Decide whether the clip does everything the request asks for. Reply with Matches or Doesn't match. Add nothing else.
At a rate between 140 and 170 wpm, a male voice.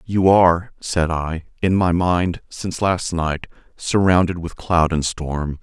Matches